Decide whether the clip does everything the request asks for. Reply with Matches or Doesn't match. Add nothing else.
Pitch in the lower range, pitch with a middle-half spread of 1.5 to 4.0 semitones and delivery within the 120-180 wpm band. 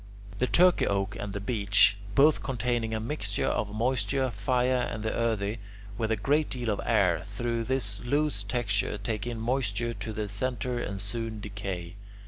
Matches